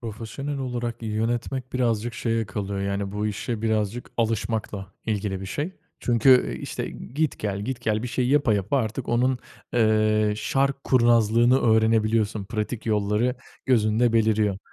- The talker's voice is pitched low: Yes, low, 115 Hz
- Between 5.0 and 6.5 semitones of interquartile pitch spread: No, narrow, 2.4 semitones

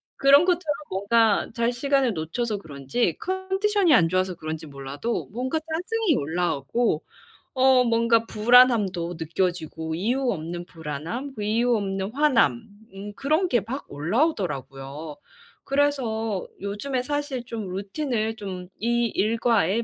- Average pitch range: No, wide, 6.7 semitones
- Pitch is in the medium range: No, high, 225 Hz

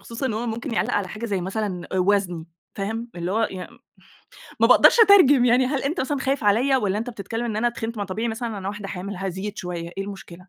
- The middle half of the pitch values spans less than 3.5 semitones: No, average, 3.8 semitones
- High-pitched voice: Yes, high, 215 Hz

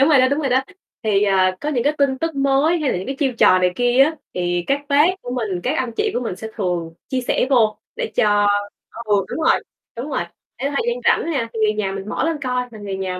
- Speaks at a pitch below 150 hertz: No, high, 245 Hz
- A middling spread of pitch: No, wide, 5.7 semitones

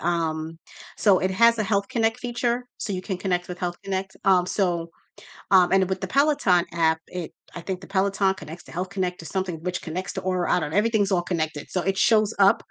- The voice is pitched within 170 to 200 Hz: Yes, medium, 185 Hz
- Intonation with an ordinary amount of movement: No, narrow, 2.3 semitones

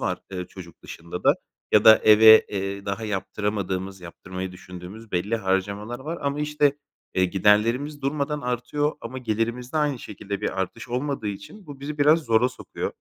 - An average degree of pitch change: No, wide, 6.2 semitones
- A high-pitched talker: No, low, 110 Hz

